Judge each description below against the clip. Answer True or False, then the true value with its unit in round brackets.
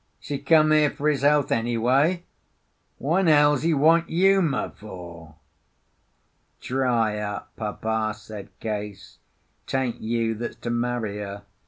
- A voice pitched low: True (120 Hz)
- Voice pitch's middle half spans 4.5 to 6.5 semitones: True (5.6 semitones)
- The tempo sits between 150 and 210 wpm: False (135 wpm)